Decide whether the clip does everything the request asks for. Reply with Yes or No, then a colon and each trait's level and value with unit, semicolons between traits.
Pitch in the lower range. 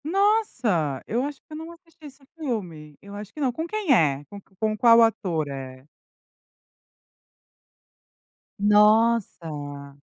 No: high, 215 Hz